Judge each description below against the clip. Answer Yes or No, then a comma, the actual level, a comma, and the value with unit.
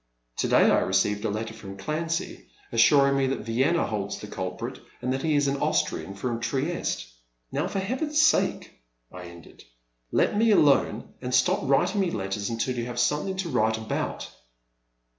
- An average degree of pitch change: No, wide, 6.1 semitones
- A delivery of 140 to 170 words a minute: No, average, 180 wpm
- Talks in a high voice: No, low, 125 Hz